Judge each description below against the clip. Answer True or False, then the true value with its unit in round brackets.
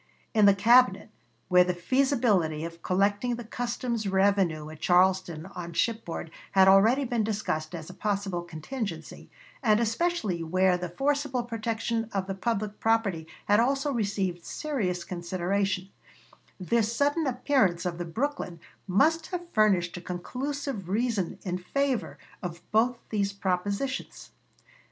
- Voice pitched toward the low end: False (200 Hz)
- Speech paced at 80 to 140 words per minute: True (135 wpm)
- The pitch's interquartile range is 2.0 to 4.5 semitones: False (5.1 semitones)